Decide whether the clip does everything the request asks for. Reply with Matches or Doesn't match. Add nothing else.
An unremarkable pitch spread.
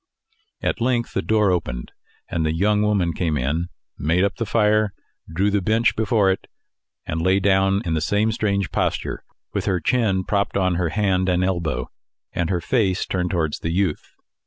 Matches